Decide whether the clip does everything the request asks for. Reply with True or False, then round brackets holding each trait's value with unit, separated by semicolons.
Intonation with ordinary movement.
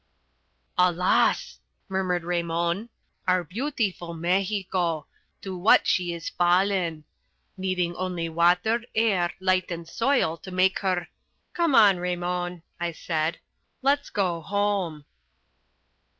False (2.3 semitones)